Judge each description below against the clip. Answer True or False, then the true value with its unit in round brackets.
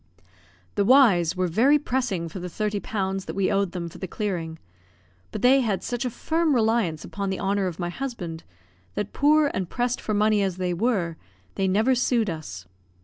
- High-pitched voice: True (200 Hz)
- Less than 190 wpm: False (200 wpm)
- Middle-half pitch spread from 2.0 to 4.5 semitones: False (5.3 semitones)